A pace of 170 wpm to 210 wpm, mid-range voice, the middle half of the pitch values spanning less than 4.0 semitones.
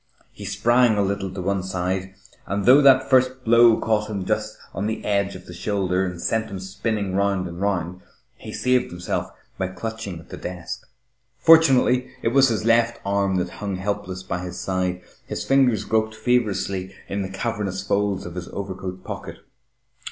No: average, 180 wpm; low, 100 Hz; average, 3.4 semitones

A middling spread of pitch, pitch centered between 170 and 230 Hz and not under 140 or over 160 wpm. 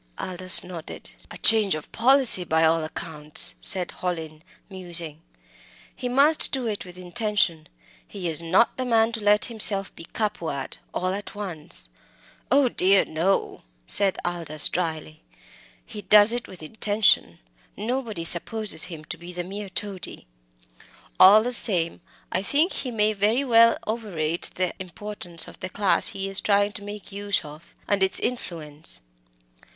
Yes: average, 4.2 semitones; high, 190 Hz; average, 155 wpm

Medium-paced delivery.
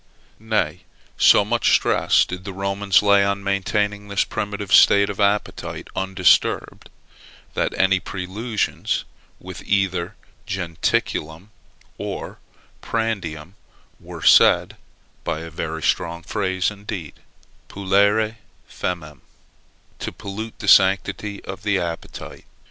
No: slow, 110 wpm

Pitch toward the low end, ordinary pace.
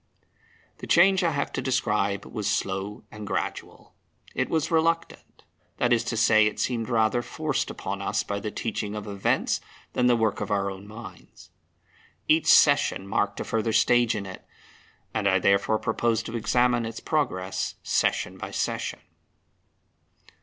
Yes: low, 110 Hz; average, 160 wpm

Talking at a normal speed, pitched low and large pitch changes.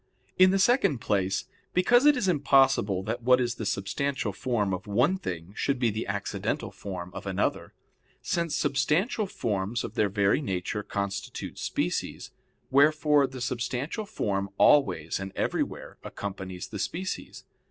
Yes: average, 145 wpm; low, 120 Hz; wide, 7.0 semitones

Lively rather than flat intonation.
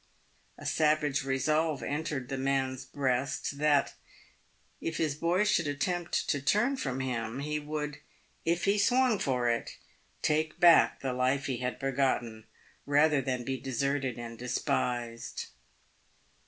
No: average, 3.2 semitones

